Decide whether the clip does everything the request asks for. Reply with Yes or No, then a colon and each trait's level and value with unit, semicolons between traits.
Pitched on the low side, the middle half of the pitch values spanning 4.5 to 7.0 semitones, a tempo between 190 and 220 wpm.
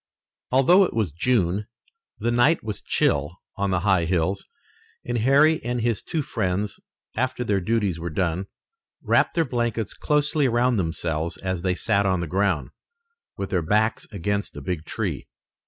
No: low, 100 Hz; average, 5.1 semitones; average, 160 wpm